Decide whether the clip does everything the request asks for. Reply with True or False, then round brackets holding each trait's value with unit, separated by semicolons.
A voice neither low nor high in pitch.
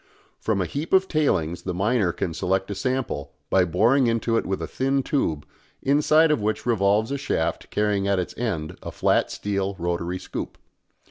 False (105 Hz)